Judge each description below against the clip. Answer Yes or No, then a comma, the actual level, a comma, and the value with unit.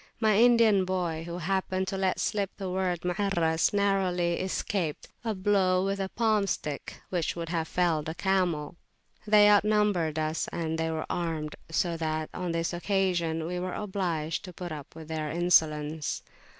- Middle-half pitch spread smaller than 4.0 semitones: Yes, average, 3.1 semitones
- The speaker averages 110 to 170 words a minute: Yes, average, 165 wpm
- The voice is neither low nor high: Yes, medium, 180 Hz